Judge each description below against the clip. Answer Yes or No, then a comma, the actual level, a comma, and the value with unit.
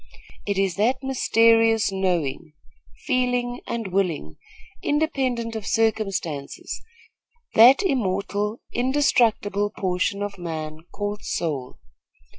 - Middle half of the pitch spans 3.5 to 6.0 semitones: Yes, average, 4.6 semitones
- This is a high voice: Yes, high, 205 Hz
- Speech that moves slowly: Yes, slow, 90 wpm